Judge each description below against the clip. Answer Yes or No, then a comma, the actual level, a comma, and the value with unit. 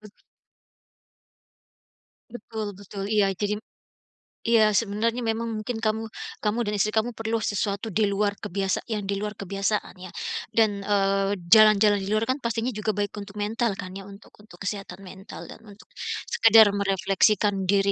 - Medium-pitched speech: No, high, 210 Hz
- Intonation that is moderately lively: No, narrow, 1.8 semitones